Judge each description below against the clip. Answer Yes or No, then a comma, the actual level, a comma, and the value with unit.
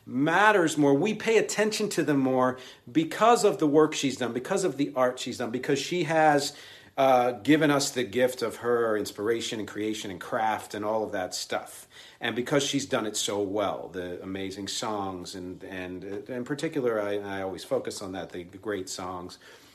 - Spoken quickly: No, average, 195 wpm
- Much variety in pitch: Yes, wide, 6.5 semitones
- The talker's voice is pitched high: No, low, 125 Hz